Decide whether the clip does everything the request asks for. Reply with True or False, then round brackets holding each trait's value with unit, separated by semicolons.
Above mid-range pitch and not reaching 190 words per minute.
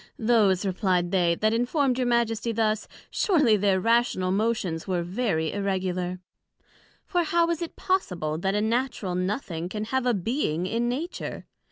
True (215 Hz; 155 wpm)